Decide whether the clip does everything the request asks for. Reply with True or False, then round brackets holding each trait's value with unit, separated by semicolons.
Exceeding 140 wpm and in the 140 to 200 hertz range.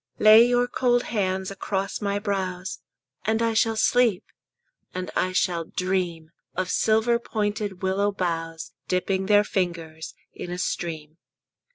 False (135 wpm; 190 Hz)